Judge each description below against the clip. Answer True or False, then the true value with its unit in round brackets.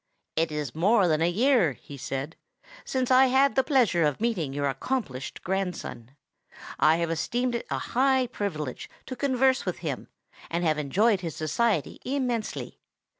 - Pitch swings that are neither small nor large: False (8.5 semitones)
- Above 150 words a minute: True (160 wpm)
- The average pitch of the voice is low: False (190 Hz)